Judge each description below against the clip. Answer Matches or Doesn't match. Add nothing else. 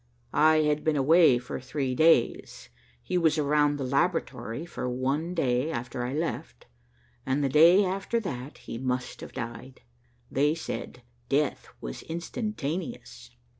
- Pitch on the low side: Doesn't match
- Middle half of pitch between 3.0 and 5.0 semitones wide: Matches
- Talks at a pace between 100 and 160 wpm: Matches